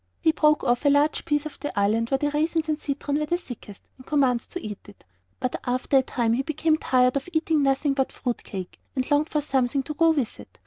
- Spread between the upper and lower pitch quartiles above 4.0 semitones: No, average, 3.3 semitones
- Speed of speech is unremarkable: No, fast, 235 wpm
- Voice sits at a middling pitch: No, very high, 280 Hz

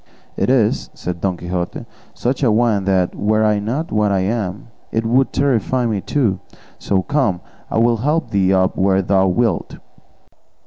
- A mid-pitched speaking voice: No, low, 105 Hz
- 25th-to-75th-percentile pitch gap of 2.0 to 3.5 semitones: No, average, 4.1 semitones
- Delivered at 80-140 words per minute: No, average, 170 wpm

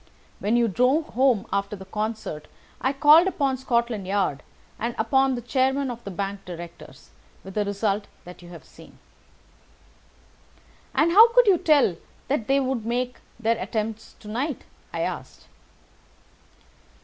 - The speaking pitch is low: No, high, 235 Hz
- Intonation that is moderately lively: Yes, average, 4.9 semitones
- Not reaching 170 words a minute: Yes, average, 150 wpm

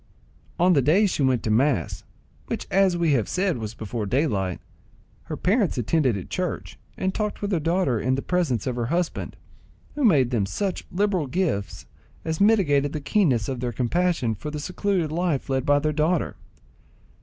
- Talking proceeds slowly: No, average, 180 wpm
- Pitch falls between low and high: Yes, medium, 150 Hz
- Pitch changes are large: Yes, wide, 6.6 semitones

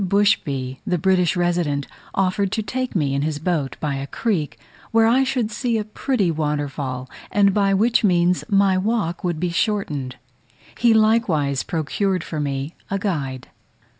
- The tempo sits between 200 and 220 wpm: No, average, 160 wpm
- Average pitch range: No, wide, 5.9 semitones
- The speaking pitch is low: No, medium, 180 Hz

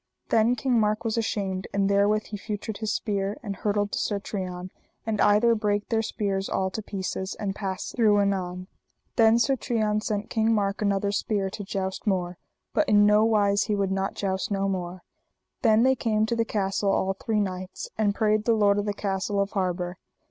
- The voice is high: Yes, high, 205 Hz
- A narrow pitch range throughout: Yes, narrow, 1.9 semitones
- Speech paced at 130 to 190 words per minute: No, average, 200 wpm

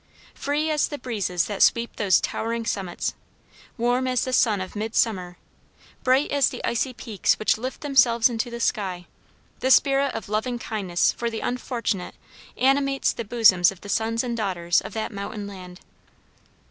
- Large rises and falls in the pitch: No, average, 4.1 semitones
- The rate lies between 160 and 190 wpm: Yes, average, 165 wpm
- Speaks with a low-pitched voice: No, high, 230 Hz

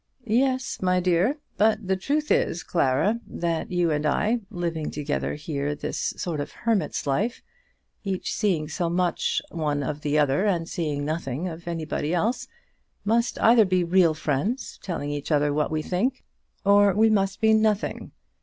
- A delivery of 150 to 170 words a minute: Yes, average, 160 wpm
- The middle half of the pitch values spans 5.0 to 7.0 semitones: Yes, wide, 5.6 semitones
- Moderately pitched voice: Yes, medium, 175 Hz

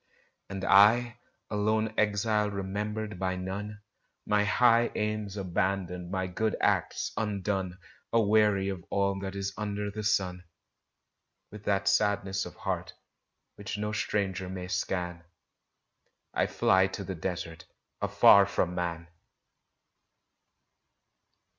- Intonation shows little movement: Yes, narrow, 2.1 semitones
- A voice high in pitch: No, low, 100 Hz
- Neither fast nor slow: No, slow, 115 wpm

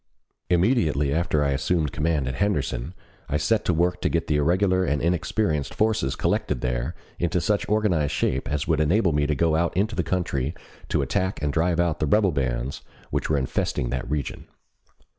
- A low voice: Yes, very low, 80 Hz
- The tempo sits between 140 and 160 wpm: No, average, 185 wpm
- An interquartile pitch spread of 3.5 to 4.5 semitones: Yes, average, 4.1 semitones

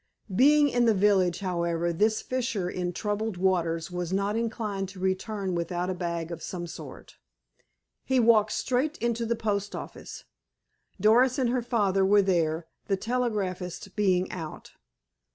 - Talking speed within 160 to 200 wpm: No, average, 150 wpm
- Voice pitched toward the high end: Yes, high, 195 Hz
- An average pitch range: Yes, average, 4.1 semitones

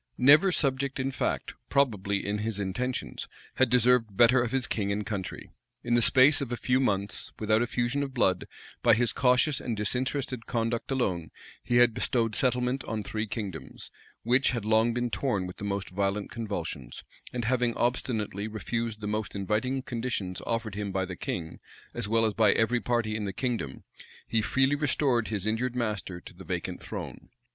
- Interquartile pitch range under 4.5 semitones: Yes, average, 3.4 semitones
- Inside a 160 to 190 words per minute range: Yes, average, 180 wpm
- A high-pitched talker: No, low, 115 Hz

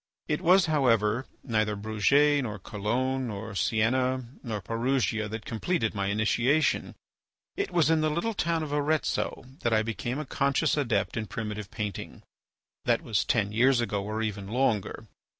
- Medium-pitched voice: No, low, 115 Hz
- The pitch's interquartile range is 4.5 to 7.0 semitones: Yes, average, 4.9 semitones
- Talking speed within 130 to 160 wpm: Yes, average, 155 wpm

